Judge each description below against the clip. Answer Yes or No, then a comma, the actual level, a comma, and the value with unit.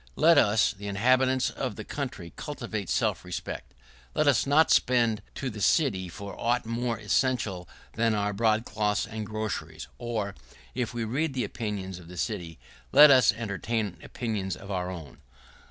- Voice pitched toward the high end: No, low, 110 Hz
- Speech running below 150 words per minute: No, average, 160 wpm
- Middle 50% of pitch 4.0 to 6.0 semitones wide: No, average, 3.6 semitones